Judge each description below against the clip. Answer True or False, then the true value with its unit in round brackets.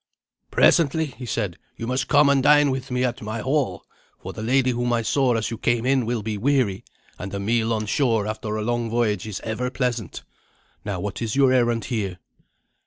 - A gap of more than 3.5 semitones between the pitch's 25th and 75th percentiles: False (3.2 semitones)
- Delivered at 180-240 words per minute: True (205 wpm)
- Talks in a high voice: False (120 Hz)